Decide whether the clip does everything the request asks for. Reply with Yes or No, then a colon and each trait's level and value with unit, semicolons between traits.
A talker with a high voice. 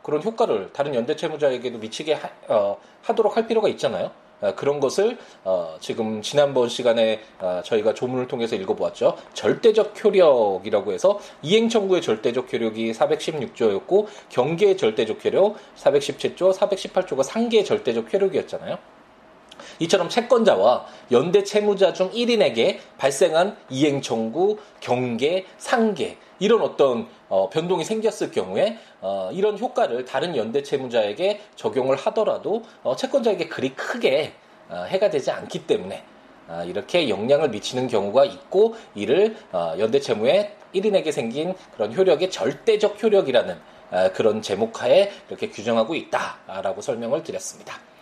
Yes: high, 195 Hz